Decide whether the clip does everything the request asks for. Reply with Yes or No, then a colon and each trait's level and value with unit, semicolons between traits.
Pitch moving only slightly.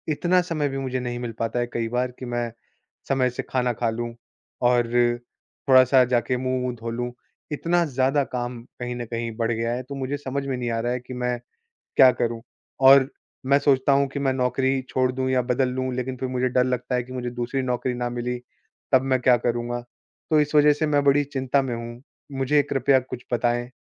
Yes: narrow, 1.7 semitones